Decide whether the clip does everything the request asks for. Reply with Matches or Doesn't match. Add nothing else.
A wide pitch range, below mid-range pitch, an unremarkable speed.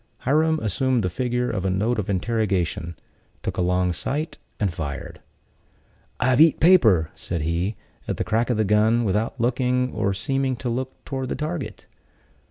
Matches